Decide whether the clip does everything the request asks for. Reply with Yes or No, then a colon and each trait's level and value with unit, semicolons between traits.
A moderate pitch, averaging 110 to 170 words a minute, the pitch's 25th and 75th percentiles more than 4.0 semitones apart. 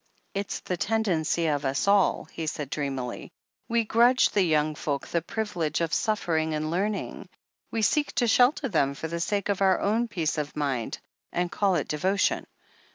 No: medium, 175 Hz; average, 180 wpm; wide, 5.4 semitones